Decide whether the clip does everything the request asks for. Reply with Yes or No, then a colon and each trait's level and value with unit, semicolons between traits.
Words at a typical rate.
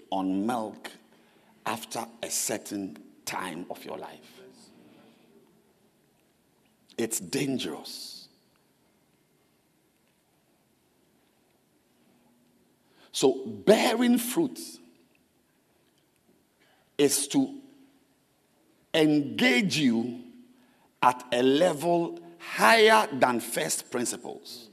No: slow, 60 wpm